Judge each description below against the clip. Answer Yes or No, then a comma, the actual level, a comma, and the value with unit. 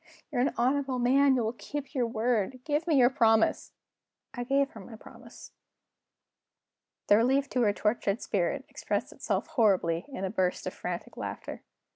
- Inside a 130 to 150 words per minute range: No, average, 165 wpm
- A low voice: No, high, 245 Hz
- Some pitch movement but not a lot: Yes, average, 4.1 semitones